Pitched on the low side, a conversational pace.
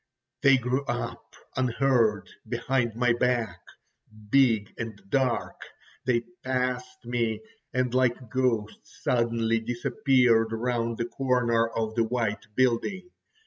No: low, 120 Hz; slow, 110 wpm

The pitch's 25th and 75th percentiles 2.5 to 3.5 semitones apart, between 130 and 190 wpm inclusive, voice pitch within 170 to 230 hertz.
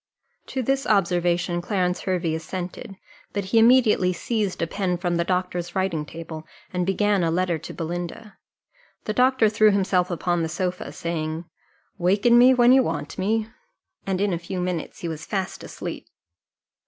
Yes: average, 3.2 semitones; average, 165 wpm; medium, 185 Hz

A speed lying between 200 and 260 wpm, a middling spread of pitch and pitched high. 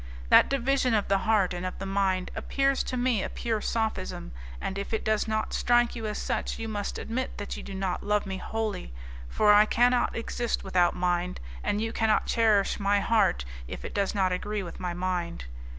Yes: fast, 205 wpm; average, 3.2 semitones; high, 205 Hz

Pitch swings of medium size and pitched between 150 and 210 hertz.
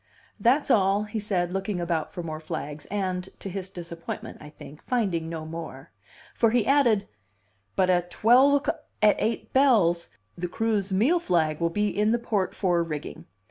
Yes: average, 4.6 semitones; high, 190 Hz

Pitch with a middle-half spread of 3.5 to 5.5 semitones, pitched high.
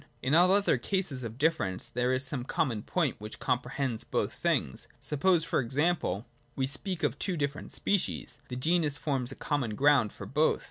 No: average, 4.6 semitones; medium, 140 Hz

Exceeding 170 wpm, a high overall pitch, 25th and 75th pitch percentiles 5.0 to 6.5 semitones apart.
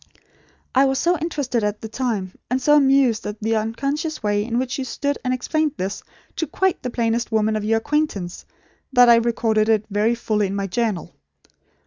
No: average, 190 wpm; high, 235 Hz; average, 4.0 semitones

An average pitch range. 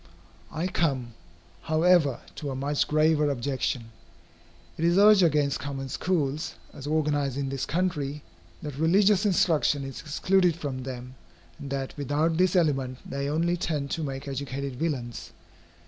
Yes: average, 3.4 semitones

